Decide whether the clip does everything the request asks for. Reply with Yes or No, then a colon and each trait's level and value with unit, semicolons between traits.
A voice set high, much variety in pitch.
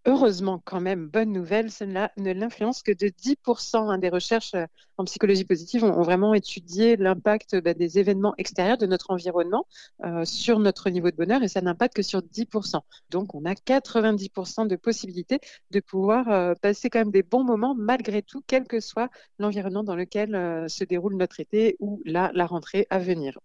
No: high, 200 Hz; average, 3.5 semitones